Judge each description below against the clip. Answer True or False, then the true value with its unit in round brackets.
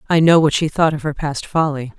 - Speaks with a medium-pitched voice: True (150 Hz)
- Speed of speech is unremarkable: False (270 wpm)